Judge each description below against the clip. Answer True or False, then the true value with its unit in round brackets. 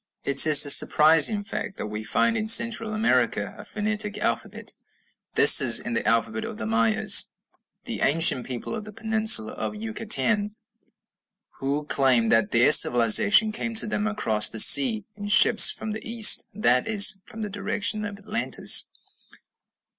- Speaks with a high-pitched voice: True (205 Hz)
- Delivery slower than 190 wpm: True (160 wpm)